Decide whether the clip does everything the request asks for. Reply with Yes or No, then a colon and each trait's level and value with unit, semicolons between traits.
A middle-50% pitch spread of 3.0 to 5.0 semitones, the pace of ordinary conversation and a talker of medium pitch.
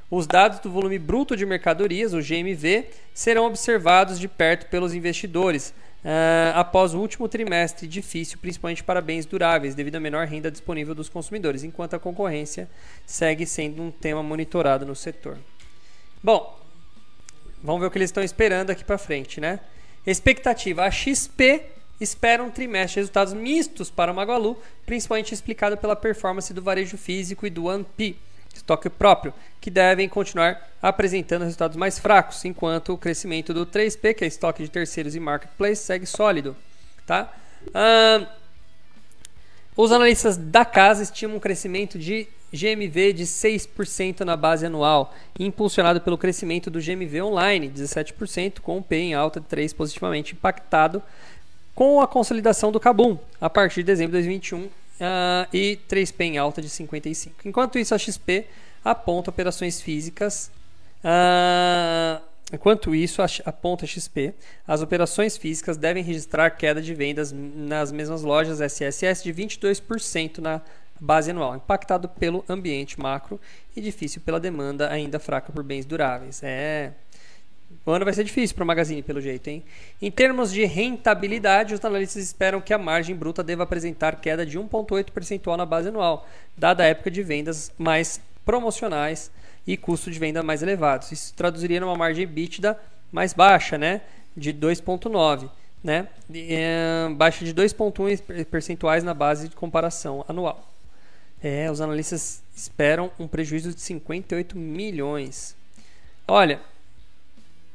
Yes: average, 4.0 semitones; average, 150 wpm; medium, 175 Hz